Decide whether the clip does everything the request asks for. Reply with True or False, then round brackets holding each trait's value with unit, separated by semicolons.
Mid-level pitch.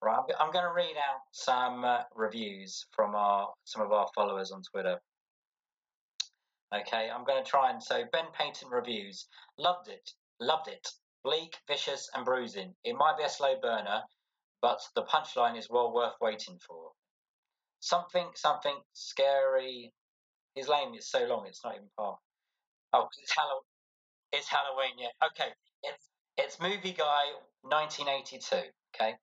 True (145 Hz)